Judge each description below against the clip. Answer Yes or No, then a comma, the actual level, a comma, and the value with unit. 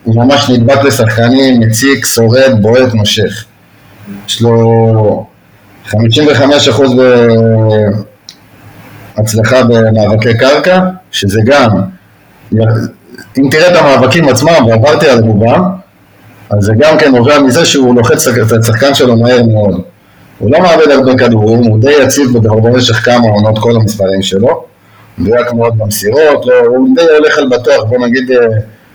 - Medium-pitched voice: No, low, 115 Hz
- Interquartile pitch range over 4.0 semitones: No, average, 3.5 semitones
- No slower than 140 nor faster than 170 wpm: No, average, 130 wpm